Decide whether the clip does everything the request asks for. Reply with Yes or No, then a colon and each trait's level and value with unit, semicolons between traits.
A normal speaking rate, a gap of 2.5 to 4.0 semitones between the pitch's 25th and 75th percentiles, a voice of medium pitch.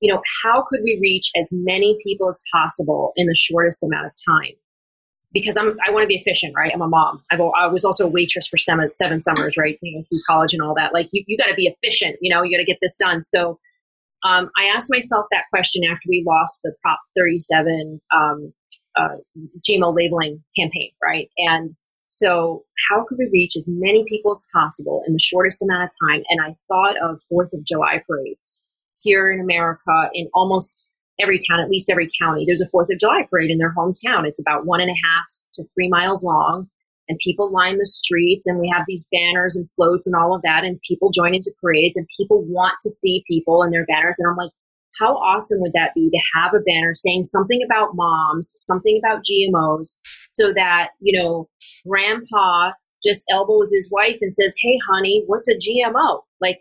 No: fast, 210 wpm; average, 3.0 semitones; medium, 180 Hz